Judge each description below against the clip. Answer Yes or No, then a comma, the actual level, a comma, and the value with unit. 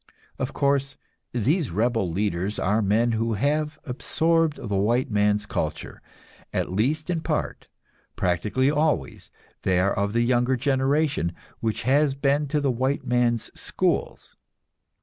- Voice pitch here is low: Yes, low, 125 Hz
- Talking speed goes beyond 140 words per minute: No, slow, 135 wpm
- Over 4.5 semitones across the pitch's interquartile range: Yes, average, 5.3 semitones